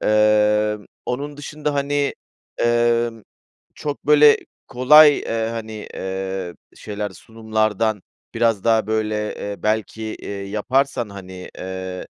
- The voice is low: Yes, low, 110 Hz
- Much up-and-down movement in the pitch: No, average, 2.9 semitones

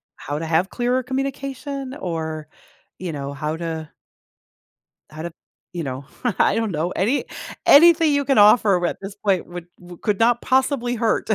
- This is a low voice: No, high, 195 Hz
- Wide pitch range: Yes, wide, 7.9 semitones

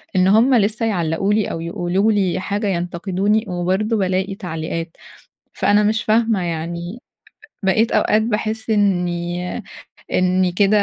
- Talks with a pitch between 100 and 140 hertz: No, high, 190 Hz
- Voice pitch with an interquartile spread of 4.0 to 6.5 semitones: No, average, 3.4 semitones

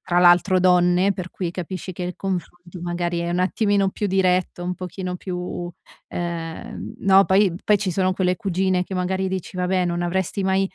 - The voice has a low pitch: No, medium, 180 Hz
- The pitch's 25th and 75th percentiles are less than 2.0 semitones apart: Yes, narrow, 1.3 semitones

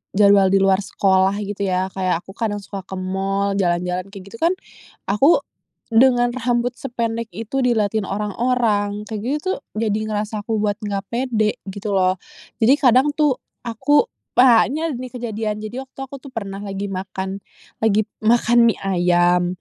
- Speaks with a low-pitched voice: No, high, 210 Hz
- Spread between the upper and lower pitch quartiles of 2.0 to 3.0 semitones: No, average, 3.6 semitones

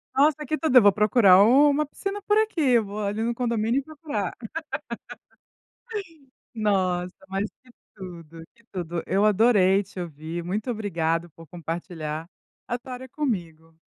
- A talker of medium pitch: No, high, 205 Hz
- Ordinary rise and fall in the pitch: No, wide, 6.3 semitones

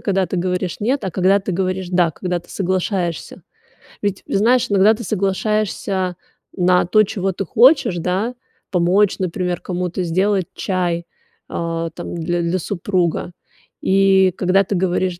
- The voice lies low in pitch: No, medium, 185 Hz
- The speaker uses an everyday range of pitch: No, narrow, 1.9 semitones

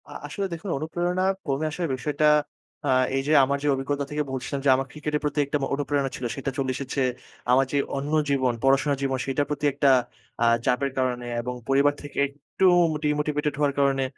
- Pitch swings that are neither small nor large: No, narrow, 1.7 semitones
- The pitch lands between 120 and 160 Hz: Yes, medium, 140 Hz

